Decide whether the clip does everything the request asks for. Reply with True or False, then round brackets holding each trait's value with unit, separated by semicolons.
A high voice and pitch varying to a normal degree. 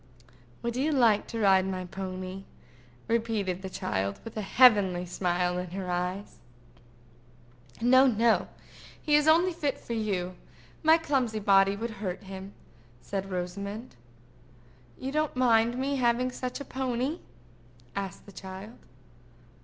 True (210 Hz; 5.0 semitones)